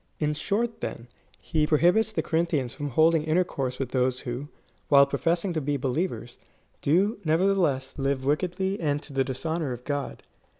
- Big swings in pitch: No, average, 4.2 semitones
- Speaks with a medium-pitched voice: Yes, medium, 150 Hz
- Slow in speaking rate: No, average, 160 wpm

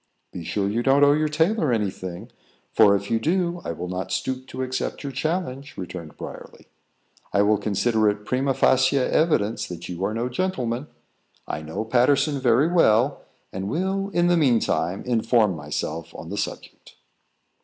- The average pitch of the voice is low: Yes, low, 120 Hz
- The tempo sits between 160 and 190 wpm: Yes, average, 175 wpm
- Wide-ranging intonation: Yes, wide, 6.1 semitones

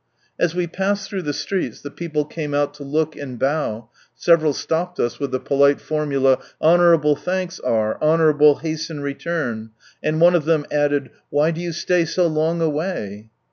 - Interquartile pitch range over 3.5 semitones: No, average, 2.9 semitones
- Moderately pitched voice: Yes, medium, 155 Hz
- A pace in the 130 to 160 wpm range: No, average, 180 wpm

